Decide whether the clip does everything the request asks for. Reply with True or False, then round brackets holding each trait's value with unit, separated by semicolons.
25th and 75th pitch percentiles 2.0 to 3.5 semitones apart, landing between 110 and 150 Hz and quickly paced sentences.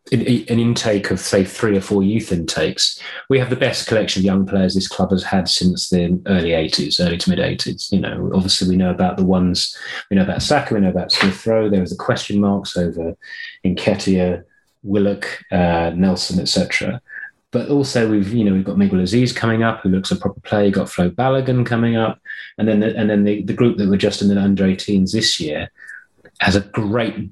False (3.1 semitones; 100 Hz; 215 wpm)